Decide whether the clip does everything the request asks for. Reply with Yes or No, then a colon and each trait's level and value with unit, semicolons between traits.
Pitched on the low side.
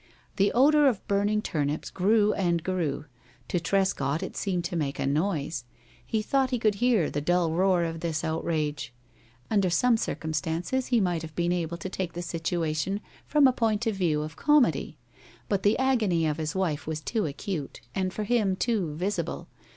No: medium, 180 Hz